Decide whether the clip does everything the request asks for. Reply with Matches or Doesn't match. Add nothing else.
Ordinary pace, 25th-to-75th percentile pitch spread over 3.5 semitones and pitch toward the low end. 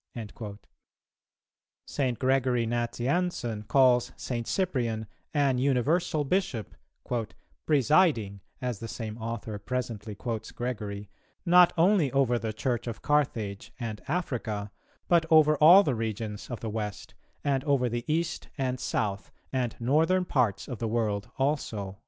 Doesn't match